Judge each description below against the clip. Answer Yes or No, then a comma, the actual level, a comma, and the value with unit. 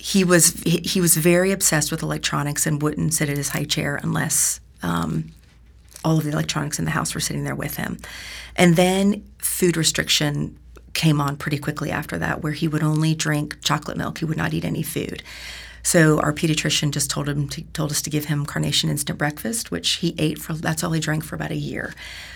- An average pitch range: No, narrow, 2.3 semitones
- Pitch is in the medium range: Yes, medium, 150 Hz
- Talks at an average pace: No, fast, 210 wpm